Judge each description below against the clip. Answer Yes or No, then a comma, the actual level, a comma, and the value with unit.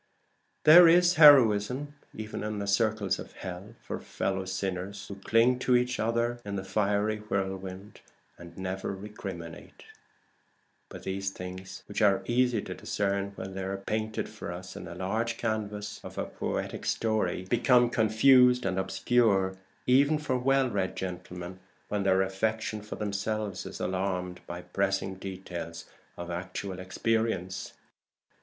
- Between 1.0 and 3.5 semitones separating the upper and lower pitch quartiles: Yes, average, 3.1 semitones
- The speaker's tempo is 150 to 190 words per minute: No, average, 140 wpm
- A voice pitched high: No, low, 100 Hz